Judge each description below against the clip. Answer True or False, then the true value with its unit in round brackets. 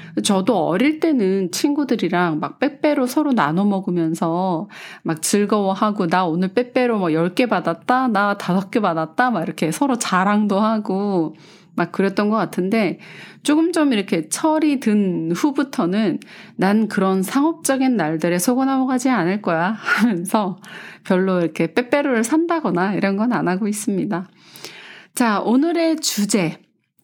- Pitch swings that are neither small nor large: False (5.7 semitones)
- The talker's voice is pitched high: True (205 Hz)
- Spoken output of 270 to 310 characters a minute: True (285 characters per minute)